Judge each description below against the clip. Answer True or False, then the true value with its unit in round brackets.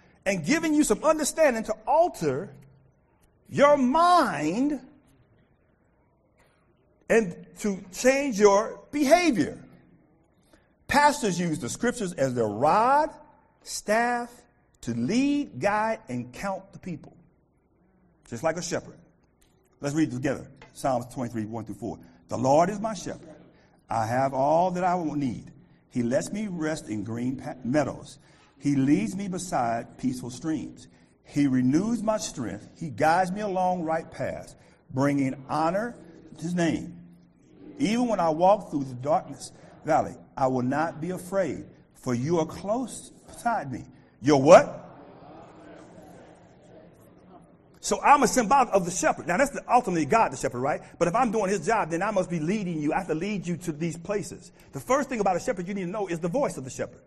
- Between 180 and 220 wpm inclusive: False (165 wpm)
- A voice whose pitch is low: False (180 Hz)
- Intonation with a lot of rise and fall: True (7.3 semitones)